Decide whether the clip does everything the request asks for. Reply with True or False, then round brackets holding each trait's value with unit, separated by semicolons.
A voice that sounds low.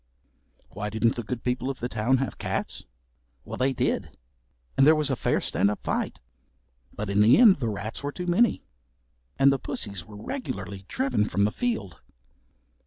True (120 Hz)